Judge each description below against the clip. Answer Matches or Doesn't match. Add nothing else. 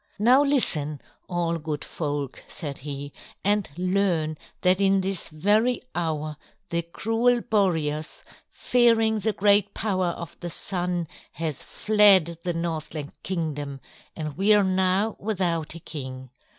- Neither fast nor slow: Doesn't match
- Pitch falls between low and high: Matches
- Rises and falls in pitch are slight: Doesn't match